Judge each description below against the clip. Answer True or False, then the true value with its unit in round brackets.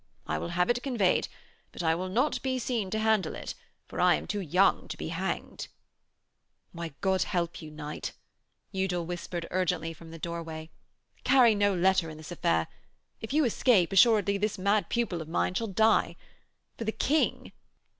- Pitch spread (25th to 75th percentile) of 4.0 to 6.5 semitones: True (4.6 semitones)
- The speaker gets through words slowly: False (175 wpm)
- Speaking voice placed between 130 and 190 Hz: True (185 Hz)